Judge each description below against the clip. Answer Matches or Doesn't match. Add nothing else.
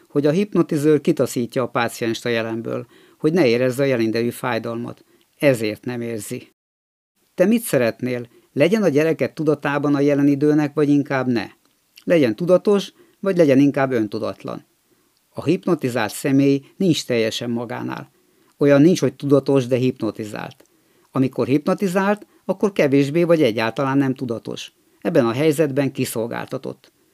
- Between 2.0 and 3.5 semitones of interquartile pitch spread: Doesn't match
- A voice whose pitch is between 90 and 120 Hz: Doesn't match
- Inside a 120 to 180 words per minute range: Matches